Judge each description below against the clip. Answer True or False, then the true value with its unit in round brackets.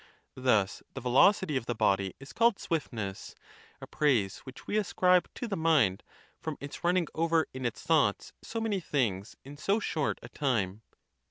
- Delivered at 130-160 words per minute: False (170 wpm)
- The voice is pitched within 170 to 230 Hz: False (140 Hz)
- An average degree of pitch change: False (7.1 semitones)